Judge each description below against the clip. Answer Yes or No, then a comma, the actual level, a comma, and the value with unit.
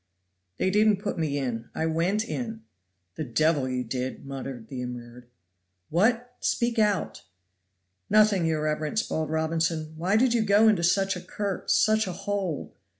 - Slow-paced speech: No, average, 160 wpm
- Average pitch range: No, wide, 6.1 semitones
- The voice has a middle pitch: Yes, medium, 170 Hz